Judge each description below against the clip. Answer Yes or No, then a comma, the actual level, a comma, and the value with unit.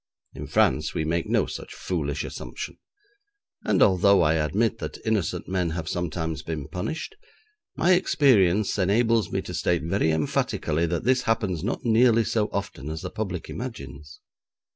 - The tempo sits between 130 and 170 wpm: Yes, average, 155 wpm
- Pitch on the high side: No, very low, 90 Hz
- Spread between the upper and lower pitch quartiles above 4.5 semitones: Yes, wide, 5.6 semitones